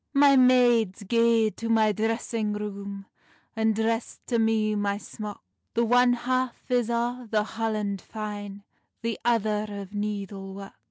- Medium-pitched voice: No, high, 220 Hz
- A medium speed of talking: Yes, average, 145 wpm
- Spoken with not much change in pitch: Yes, narrow, 2.3 semitones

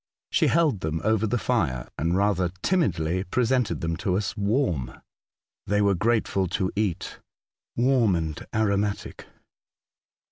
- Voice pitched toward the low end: Yes, low, 100 Hz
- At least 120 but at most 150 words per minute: Yes, slow, 135 wpm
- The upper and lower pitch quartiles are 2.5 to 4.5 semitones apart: Yes, average, 4.1 semitones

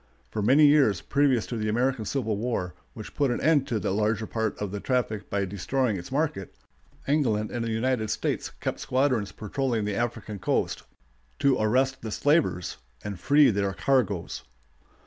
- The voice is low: Yes, low, 115 Hz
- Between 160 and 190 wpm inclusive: Yes, average, 170 wpm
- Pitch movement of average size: Yes, average, 4.4 semitones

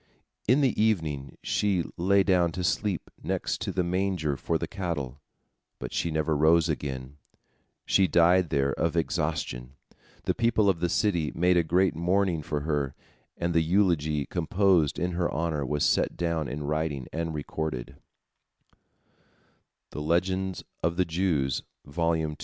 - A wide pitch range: No, average, 3.4 semitones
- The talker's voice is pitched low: Yes, very low, 85 Hz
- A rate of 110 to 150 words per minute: Yes, slow, 135 wpm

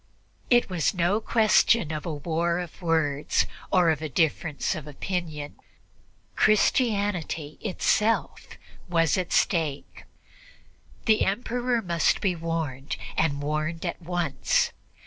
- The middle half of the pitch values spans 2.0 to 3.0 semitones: No, average, 4.2 semitones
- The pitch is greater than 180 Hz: No, medium, 170 Hz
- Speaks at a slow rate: Yes, slow, 110 wpm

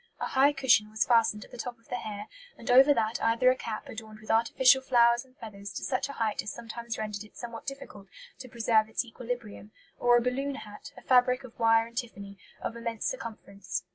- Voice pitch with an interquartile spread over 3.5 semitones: No, narrow, 2.6 semitones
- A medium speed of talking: No, fast, 215 wpm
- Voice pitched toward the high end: Yes, high, 230 Hz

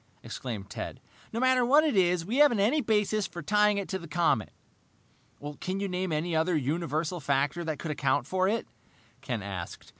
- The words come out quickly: No, average, 185 wpm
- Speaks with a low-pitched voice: No, medium, 175 Hz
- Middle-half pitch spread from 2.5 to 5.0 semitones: No, wide, 5.6 semitones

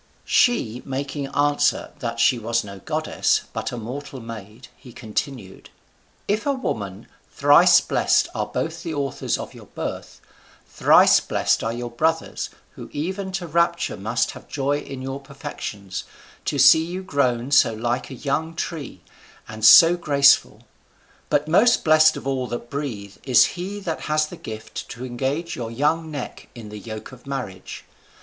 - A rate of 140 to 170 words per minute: Yes, average, 160 wpm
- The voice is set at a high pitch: No, low, 135 Hz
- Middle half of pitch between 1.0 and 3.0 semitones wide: No, average, 5.1 semitones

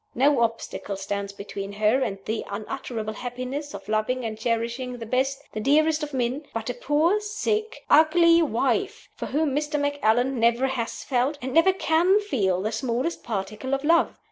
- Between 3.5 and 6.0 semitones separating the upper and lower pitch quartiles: Yes, average, 5.0 semitones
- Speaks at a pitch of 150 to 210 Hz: No, very high, 255 Hz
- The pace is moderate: Yes, average, 170 wpm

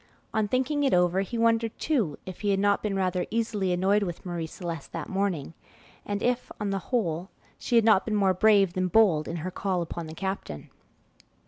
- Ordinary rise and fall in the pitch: Yes, average, 3.6 semitones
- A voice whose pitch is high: Yes, high, 195 Hz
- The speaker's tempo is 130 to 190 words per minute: No, fast, 205 wpm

